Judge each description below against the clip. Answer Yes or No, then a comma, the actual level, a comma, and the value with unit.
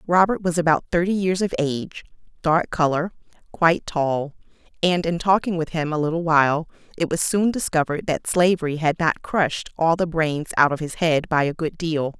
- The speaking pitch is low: No, medium, 165 Hz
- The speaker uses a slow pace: No, average, 190 wpm